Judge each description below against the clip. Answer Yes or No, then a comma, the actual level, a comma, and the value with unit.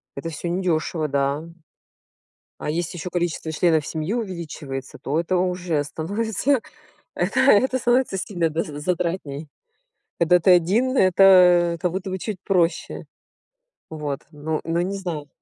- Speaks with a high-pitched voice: No, medium, 175 Hz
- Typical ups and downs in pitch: Yes, average, 3.2 semitones